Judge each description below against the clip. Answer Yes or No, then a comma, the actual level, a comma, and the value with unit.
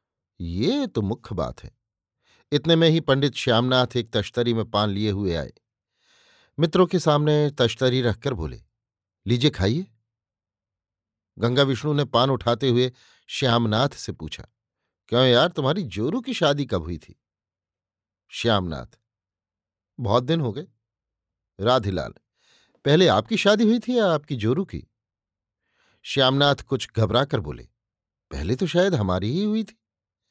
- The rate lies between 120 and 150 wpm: Yes, average, 140 wpm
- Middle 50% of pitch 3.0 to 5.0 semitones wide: No, wide, 5.6 semitones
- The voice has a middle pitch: No, low, 120 Hz